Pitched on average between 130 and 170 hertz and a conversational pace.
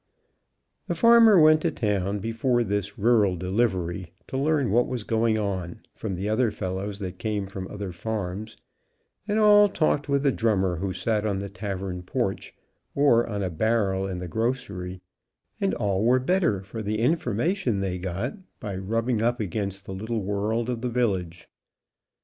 No: low, 105 Hz; average, 165 wpm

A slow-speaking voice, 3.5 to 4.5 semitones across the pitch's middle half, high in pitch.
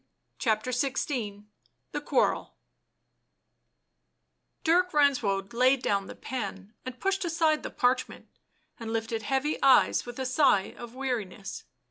Yes: slow, 120 wpm; average, 4.0 semitones; very high, 250 Hz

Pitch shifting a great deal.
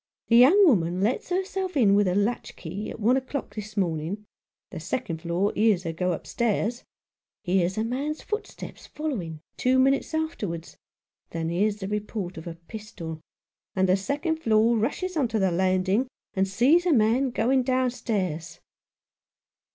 Yes: wide, 5.9 semitones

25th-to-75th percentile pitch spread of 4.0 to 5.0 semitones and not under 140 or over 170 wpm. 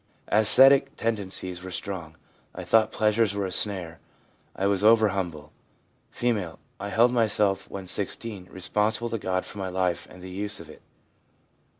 No: average, 3.0 semitones; average, 160 wpm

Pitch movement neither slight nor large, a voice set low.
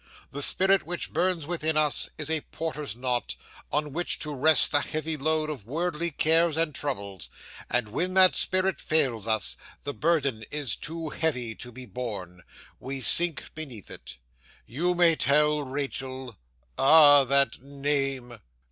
No: average, 3.9 semitones; medium, 145 Hz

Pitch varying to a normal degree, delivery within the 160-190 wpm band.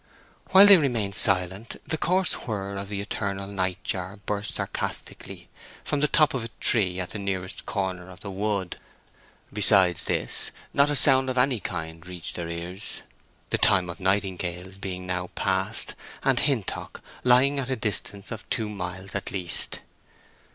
Yes: average, 4.4 semitones; average, 165 wpm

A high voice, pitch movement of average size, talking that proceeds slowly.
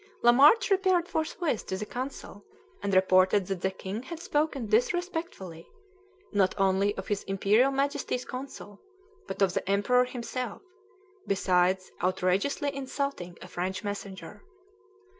No: high, 205 Hz; wide, 6.5 semitones; slow, 125 wpm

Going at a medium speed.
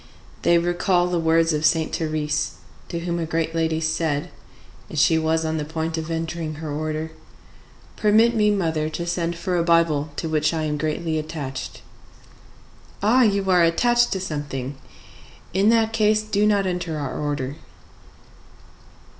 Yes: average, 160 wpm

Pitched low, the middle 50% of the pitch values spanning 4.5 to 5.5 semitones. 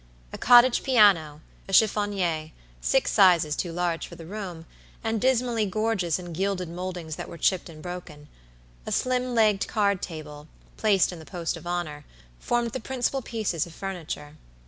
No: medium, 185 Hz; average, 4.9 semitones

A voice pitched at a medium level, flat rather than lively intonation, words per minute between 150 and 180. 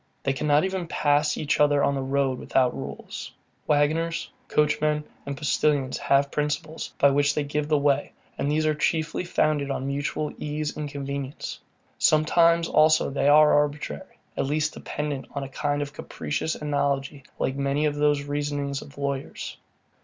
Yes: medium, 145 Hz; narrow, 1.4 semitones; average, 160 wpm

